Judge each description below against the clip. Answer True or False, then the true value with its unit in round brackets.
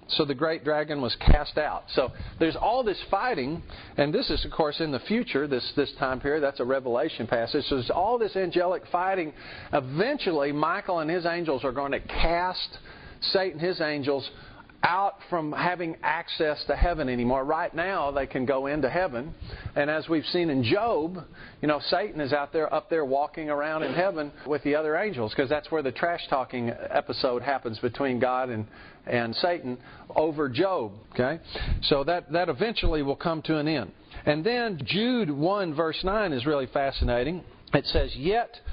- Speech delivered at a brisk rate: False (185 wpm)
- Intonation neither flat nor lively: True (4.1 semitones)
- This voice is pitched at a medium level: True (150 Hz)